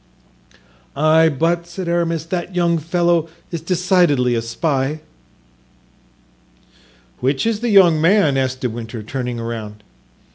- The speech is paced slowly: Yes, slow, 120 wpm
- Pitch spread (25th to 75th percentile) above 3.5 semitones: Yes, average, 5.0 semitones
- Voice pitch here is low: No, medium, 160 Hz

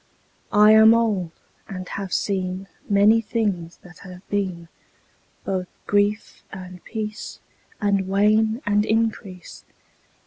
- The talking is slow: Yes, slow, 110 wpm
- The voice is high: Yes, high, 200 Hz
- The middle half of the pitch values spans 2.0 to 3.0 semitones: Yes, average, 2.7 semitones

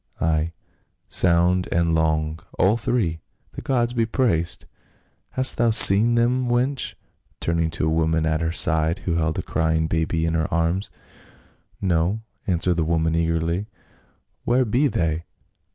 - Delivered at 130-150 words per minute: Yes, average, 145 wpm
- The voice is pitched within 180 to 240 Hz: No, very low, 85 Hz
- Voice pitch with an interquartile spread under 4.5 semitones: No, wide, 5.4 semitones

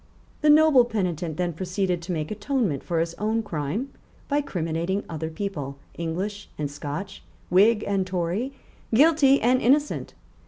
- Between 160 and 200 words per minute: No, average, 145 wpm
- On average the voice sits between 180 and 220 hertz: Yes, high, 190 Hz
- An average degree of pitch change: No, wide, 6.0 semitones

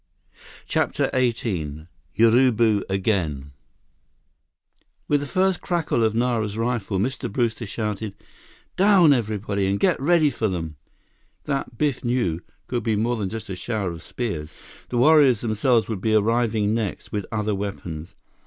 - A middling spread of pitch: Yes, average, 3.7 semitones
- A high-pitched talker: No, low, 110 Hz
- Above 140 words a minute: No, slow, 135 wpm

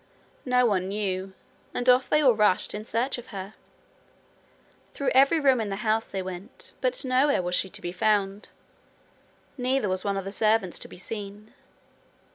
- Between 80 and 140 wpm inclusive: No, average, 175 wpm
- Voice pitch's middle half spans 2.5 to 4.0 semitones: No, average, 4.5 semitones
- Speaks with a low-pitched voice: No, high, 215 Hz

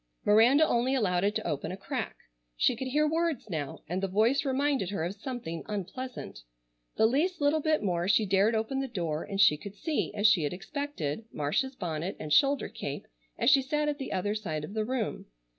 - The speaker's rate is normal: No, fast, 210 wpm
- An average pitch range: No, wide, 7.0 semitones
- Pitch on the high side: Yes, high, 215 Hz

